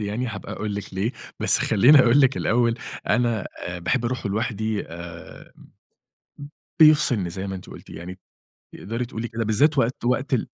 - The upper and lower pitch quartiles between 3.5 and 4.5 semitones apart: Yes, average, 3.9 semitones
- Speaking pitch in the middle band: No, low, 115 Hz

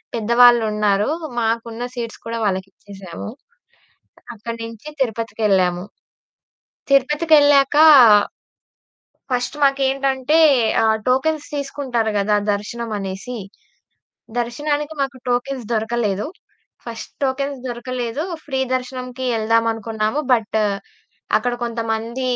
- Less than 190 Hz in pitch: No, high, 235 Hz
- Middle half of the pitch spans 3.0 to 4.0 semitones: Yes, average, 3.3 semitones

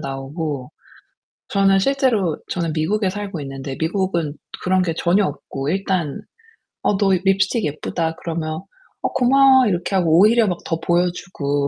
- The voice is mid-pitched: Yes, medium, 180 Hz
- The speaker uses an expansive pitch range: No, average, 4.0 semitones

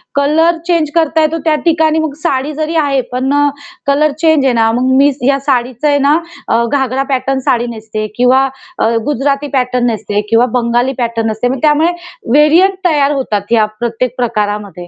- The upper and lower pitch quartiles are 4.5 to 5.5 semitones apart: No, average, 4.1 semitones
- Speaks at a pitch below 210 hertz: No, very high, 270 Hz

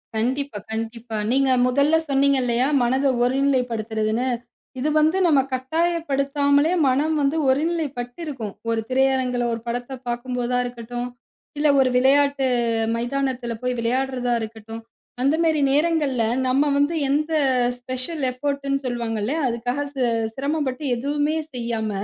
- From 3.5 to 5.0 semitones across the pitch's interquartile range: No, average, 2.8 semitones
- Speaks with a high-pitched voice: Yes, very high, 260 Hz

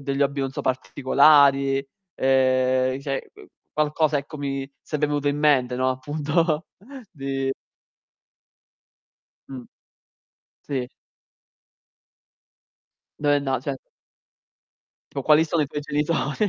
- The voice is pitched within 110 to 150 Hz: Yes, medium, 140 Hz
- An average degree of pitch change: No, narrow, 1.9 semitones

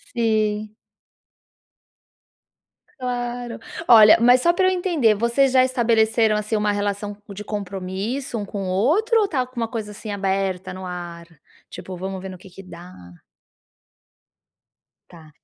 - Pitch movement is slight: No, average, 4.1 semitones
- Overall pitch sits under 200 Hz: No, high, 215 Hz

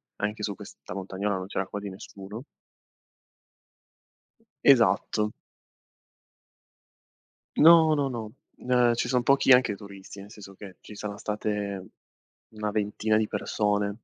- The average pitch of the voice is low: Yes, low, 105 Hz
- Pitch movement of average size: No, narrow, 1.8 semitones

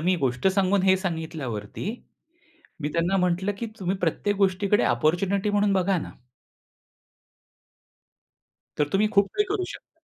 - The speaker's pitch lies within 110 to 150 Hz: No, high, 190 Hz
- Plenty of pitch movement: No, average, 3.2 semitones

